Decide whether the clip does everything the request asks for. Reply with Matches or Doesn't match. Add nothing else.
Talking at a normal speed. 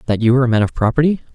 Doesn't match